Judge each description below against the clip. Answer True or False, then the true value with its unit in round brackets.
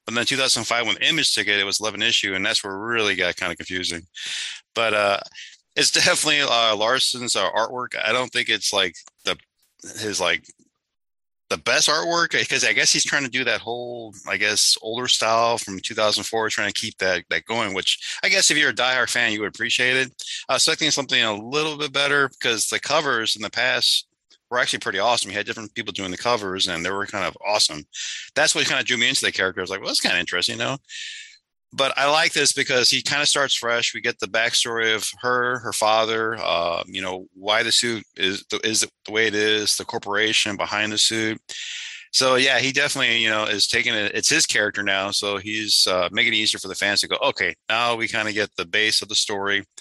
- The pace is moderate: False (235 wpm)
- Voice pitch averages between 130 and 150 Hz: False (110 Hz)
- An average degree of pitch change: True (3.2 semitones)